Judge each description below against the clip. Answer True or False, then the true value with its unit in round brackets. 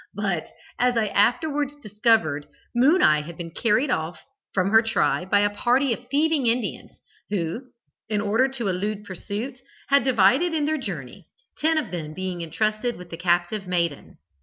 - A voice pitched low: False (215 Hz)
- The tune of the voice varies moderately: False (6.0 semitones)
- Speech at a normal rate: True (160 wpm)